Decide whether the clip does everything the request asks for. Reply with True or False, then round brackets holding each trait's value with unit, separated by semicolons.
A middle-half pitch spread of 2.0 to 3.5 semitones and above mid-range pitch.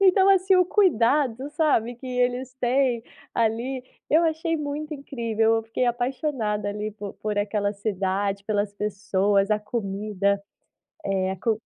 False (5.1 semitones; 225 Hz)